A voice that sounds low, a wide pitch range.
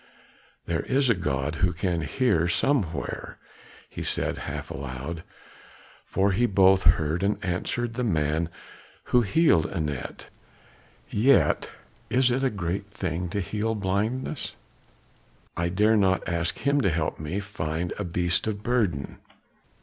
No: very low, 95 Hz; average, 4.9 semitones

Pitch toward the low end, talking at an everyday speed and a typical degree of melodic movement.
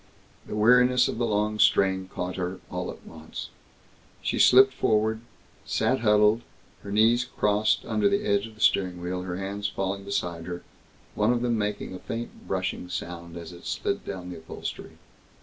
Yes: low, 105 Hz; average, 175 wpm; average, 3.6 semitones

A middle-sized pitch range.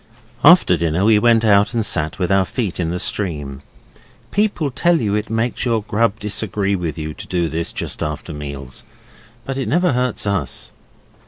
No: wide, 5.7 semitones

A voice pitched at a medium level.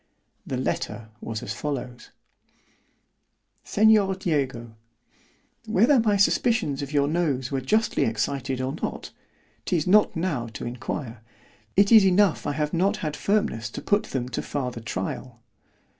Yes: medium, 145 Hz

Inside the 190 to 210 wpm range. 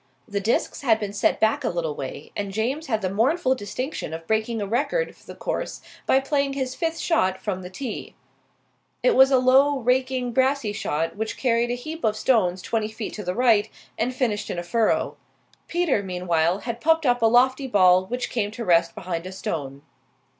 Yes: average, 200 wpm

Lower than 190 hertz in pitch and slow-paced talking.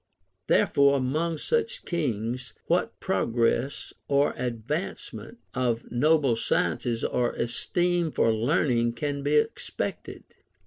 Yes: low, 135 Hz; slow, 100 wpm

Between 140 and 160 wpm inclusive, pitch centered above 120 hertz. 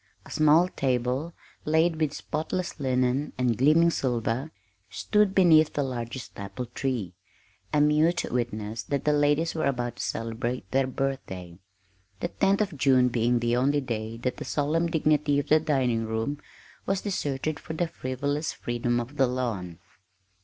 Yes: average, 155 wpm; low, 135 Hz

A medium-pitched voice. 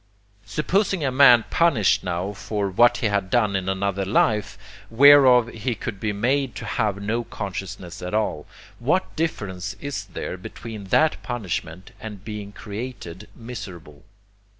No: low, 105 Hz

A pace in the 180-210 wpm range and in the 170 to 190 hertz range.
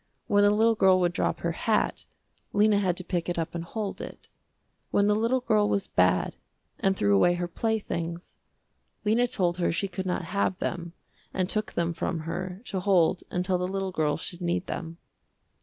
Yes: average, 190 wpm; medium, 185 Hz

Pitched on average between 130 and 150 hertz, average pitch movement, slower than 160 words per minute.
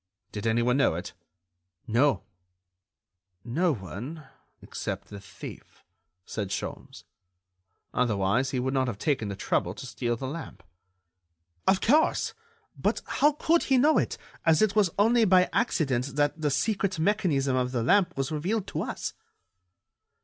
No: medium, 140 Hz; wide, 7.9 semitones; average, 140 wpm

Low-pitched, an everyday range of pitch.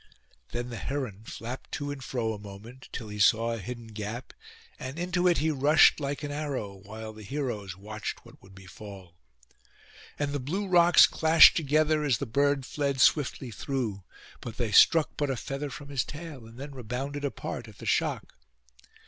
Yes: low, 130 Hz; average, 4.9 semitones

